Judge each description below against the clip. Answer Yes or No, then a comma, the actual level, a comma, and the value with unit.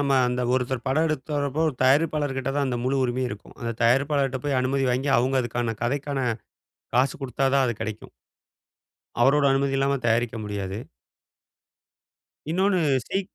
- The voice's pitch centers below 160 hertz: Yes, low, 135 Hz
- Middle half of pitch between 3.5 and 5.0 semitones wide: No, narrow, 2.6 semitones